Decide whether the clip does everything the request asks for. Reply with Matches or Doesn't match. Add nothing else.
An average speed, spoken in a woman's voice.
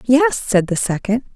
Matches